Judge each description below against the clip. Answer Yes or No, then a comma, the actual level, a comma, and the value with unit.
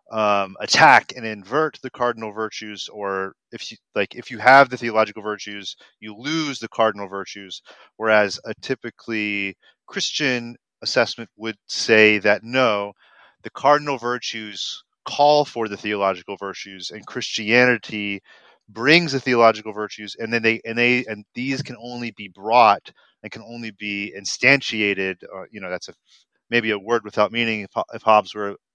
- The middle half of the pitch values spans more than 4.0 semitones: No, average, 2.9 semitones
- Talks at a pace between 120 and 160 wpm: Yes, average, 155 wpm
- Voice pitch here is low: Yes, low, 110 Hz